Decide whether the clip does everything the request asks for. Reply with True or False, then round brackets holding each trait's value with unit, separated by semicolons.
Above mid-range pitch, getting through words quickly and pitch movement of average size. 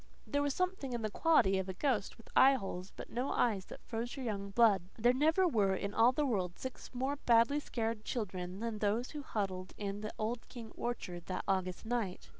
True (225 Hz; 210 wpm; 4.6 semitones)